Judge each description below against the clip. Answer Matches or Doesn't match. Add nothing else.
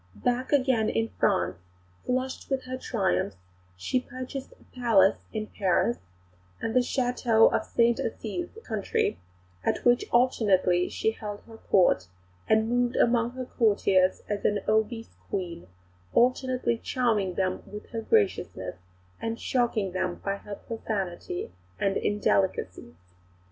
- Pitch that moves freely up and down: Doesn't match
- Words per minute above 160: Doesn't match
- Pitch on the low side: Doesn't match